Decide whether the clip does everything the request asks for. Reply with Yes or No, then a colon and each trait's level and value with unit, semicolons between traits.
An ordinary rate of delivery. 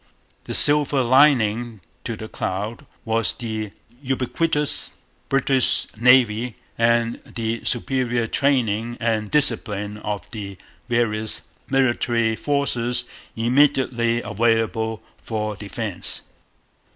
No: slow, 95 wpm